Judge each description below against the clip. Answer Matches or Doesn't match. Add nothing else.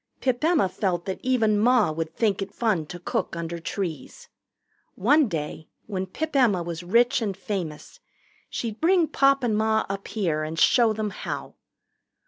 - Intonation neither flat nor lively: Doesn't match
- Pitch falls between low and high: Doesn't match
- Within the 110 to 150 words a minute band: Doesn't match